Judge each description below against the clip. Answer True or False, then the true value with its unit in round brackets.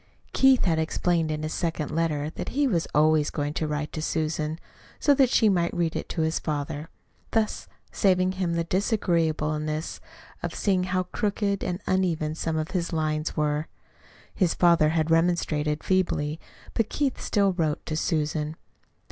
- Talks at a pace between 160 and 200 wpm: True (165 wpm)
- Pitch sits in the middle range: True (165 Hz)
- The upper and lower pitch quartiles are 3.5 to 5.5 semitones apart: False (3.1 semitones)